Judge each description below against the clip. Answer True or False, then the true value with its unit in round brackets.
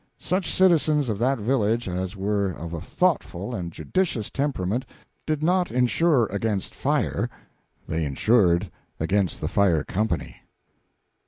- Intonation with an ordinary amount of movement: False (7.2 semitones)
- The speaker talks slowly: True (130 wpm)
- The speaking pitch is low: True (105 Hz)